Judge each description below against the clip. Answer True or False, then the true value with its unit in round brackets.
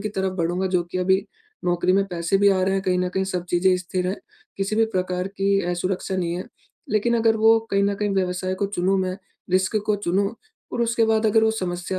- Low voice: False (190 Hz)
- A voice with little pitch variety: True (1.9 semitones)